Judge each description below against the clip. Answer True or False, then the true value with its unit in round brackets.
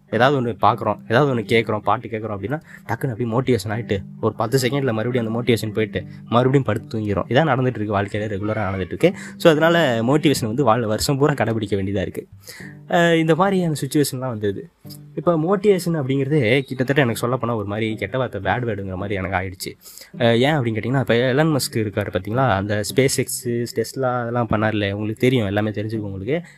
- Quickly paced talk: True (180 wpm)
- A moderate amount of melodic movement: True (4.9 semitones)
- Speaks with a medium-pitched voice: False (120 Hz)